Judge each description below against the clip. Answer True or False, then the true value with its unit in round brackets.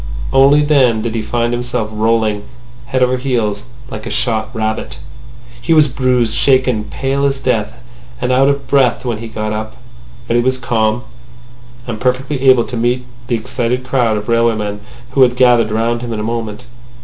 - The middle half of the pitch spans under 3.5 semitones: True (2.7 semitones)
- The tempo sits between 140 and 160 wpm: False (185 wpm)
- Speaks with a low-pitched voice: True (120 Hz)